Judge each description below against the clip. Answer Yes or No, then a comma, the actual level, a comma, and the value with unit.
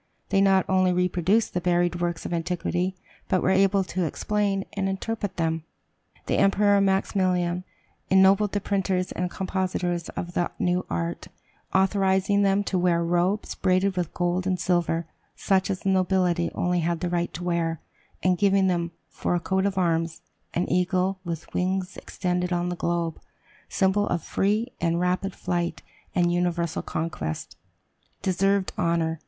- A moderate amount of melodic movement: No, narrow, 1.8 semitones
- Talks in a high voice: No, medium, 180 Hz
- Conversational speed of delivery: Yes, average, 155 wpm